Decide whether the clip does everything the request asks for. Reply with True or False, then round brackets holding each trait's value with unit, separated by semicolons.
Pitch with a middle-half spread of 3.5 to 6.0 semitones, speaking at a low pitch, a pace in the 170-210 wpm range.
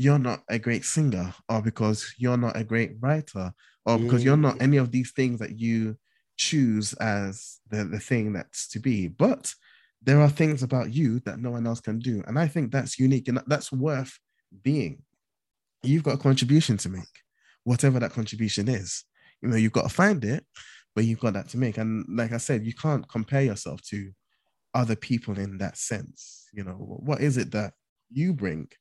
True (3.9 semitones; 120 Hz; 200 wpm)